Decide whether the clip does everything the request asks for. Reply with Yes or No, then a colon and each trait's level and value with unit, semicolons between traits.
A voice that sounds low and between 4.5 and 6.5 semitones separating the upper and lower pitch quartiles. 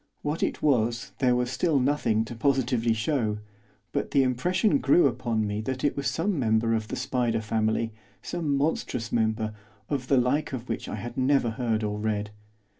No: low, 125 Hz; average, 3.9 semitones